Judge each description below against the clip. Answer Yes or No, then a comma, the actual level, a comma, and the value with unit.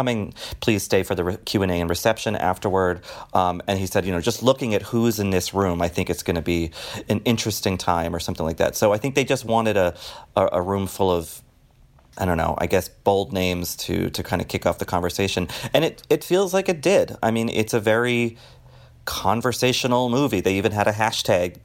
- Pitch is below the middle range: Yes, low, 100 Hz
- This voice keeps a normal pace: No, fast, 230 wpm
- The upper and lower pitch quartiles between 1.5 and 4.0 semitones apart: No, average, 4.5 semitones